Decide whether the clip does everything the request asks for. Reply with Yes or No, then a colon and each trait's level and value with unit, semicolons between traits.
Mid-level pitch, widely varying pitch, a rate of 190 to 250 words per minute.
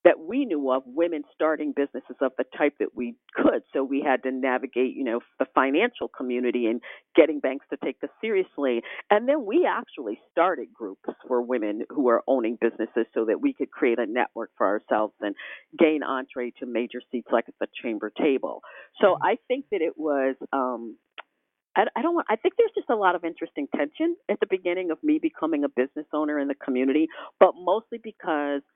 Yes: medium, 150 Hz; wide, 8.4 semitones; fast, 205 wpm